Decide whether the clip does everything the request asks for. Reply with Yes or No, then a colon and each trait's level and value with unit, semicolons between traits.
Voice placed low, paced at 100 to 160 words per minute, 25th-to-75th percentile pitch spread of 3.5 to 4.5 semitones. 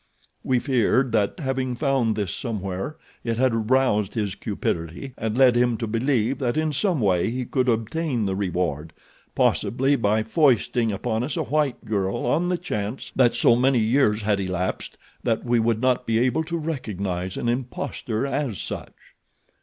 No: low, 120 Hz; average, 170 wpm; average, 4.0 semitones